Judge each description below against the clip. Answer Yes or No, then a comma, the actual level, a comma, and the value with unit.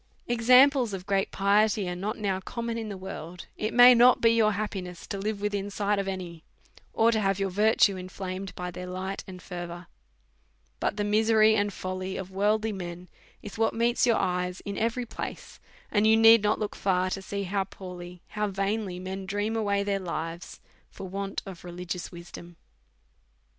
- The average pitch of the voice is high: Yes, high, 195 Hz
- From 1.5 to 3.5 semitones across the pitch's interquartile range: Yes, average, 2.8 semitones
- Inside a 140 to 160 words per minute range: No, average, 185 wpm